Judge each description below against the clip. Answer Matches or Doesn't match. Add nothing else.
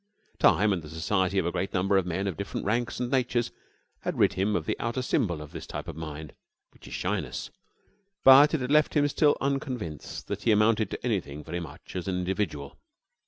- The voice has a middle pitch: Doesn't match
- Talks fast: Matches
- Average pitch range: Doesn't match